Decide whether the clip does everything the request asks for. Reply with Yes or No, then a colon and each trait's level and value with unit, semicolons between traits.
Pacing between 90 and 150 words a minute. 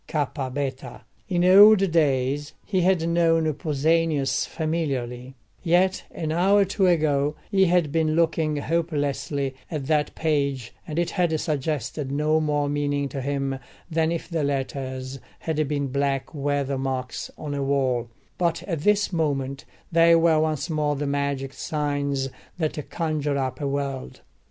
Yes: average, 145 wpm